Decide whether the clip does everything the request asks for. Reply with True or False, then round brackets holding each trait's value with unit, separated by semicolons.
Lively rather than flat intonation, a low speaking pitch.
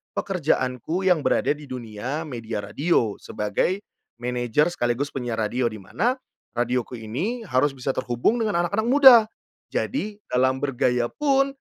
True (7.3 semitones; 130 Hz)